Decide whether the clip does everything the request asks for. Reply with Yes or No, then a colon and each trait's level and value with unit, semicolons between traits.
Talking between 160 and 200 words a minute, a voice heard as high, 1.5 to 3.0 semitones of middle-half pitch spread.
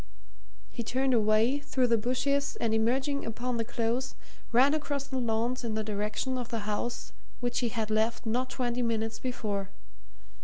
Yes: average, 165 wpm; high, 240 Hz; narrow, 2.6 semitones